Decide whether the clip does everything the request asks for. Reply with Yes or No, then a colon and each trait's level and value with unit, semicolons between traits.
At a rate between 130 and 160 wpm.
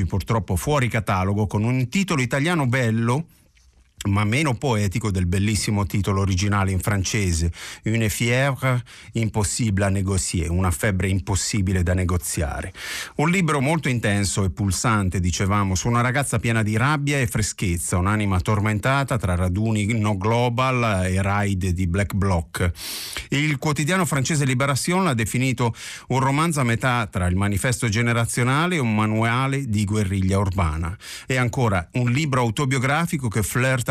Yes: average, 140 wpm